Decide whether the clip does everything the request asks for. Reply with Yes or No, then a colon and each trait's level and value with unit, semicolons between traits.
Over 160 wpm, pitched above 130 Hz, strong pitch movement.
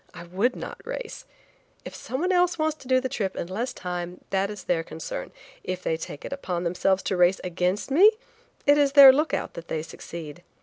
Yes: fast, 205 wpm; high, 190 Hz; wide, 7.7 semitones